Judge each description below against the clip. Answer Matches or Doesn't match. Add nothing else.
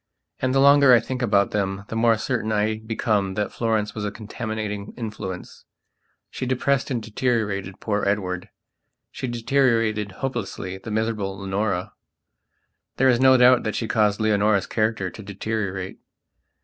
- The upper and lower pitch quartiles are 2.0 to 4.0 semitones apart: Matches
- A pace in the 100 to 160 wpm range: Matches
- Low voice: Matches